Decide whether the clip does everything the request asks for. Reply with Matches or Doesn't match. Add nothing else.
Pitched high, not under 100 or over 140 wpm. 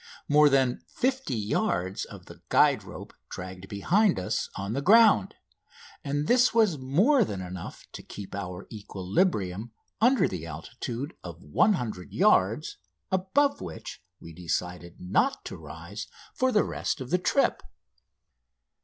Doesn't match